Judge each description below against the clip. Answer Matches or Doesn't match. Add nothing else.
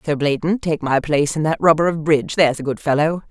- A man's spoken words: Doesn't match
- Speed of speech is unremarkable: Doesn't match